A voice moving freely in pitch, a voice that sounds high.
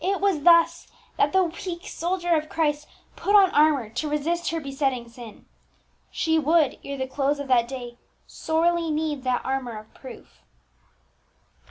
No: average, 4.3 semitones; very high, 300 Hz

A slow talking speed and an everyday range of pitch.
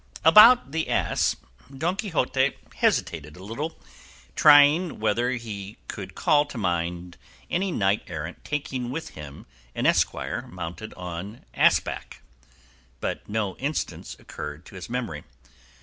No: slow, 130 wpm; wide, 8.8 semitones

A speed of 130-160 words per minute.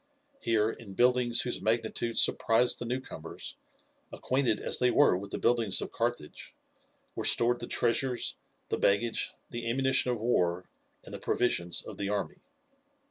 Yes: average, 150 wpm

